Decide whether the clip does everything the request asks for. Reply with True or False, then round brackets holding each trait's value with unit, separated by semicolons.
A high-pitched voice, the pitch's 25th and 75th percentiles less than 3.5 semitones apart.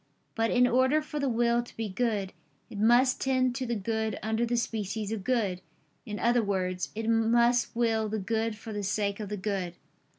True (225 Hz; 2.6 semitones)